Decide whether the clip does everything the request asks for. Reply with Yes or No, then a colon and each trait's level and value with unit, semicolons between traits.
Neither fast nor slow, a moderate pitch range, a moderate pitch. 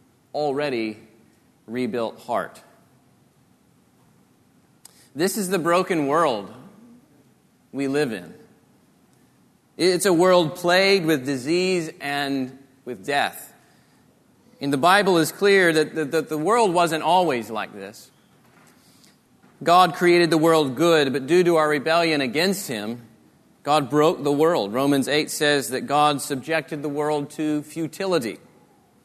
No: slow, 125 wpm; average, 3.8 semitones; medium, 155 Hz